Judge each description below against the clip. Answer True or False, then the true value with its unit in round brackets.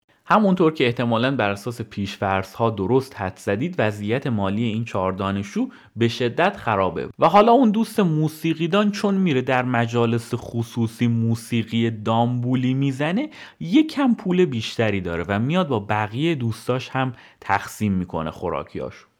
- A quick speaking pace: False (140 wpm)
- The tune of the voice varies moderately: False (6.8 semitones)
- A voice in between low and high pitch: False (120 Hz)